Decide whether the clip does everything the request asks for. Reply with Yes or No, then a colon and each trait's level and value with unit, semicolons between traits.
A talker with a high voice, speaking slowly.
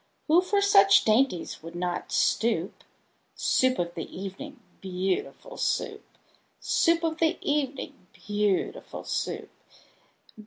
Yes: high, 215 Hz; slow, 110 wpm